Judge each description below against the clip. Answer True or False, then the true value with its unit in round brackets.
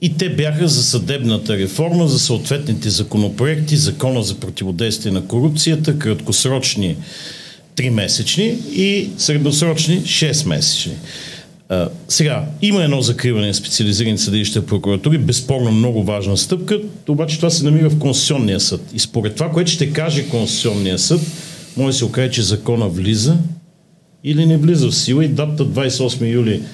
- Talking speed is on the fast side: False (140 wpm)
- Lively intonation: True (6.2 semitones)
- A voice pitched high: False (140 Hz)